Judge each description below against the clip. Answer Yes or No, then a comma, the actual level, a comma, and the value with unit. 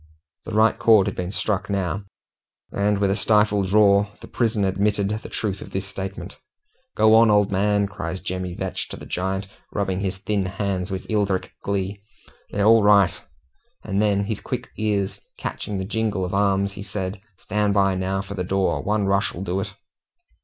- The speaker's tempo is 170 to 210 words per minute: Yes, average, 180 wpm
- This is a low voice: Yes, low, 100 Hz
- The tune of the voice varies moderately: No, narrow, 1.5 semitones